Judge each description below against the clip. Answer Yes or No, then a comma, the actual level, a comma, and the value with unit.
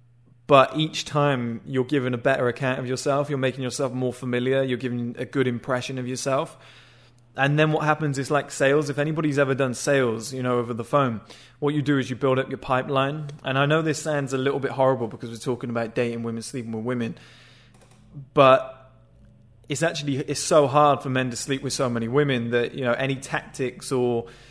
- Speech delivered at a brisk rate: Yes, fast, 210 wpm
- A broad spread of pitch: No, narrow, 2.6 semitones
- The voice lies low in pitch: Yes, low, 130 Hz